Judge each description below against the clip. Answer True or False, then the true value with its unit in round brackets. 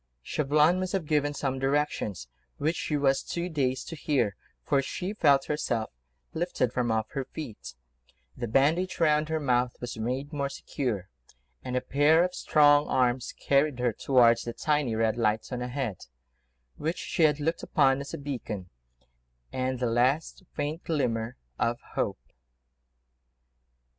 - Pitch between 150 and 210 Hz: False (135 Hz)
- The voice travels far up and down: False (3.7 semitones)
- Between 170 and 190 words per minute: False (155 wpm)